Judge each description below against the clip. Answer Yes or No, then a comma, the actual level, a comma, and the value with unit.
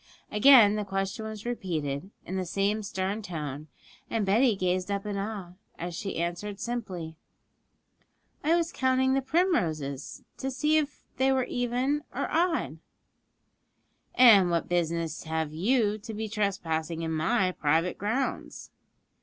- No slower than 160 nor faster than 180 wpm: No, average, 140 wpm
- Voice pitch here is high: Yes, high, 200 Hz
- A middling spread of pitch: No, wide, 6.1 semitones